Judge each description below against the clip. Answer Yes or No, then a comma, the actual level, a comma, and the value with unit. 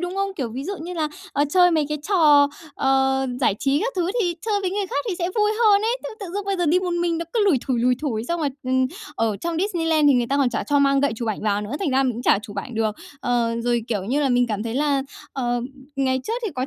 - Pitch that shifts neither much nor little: No, wide, 6.2 semitones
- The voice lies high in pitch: Yes, very high, 280 Hz